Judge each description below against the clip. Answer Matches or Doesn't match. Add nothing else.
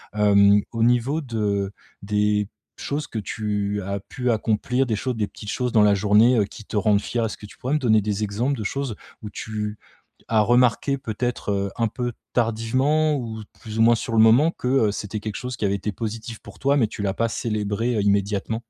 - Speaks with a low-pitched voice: Matches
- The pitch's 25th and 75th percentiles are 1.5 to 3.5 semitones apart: Matches